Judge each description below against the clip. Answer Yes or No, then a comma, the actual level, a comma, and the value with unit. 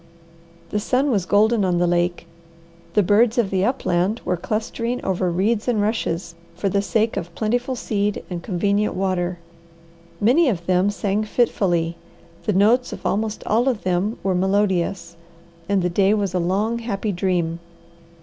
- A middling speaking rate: Yes, average, 160 wpm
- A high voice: Yes, high, 200 Hz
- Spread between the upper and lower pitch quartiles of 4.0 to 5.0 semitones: No, average, 3.4 semitones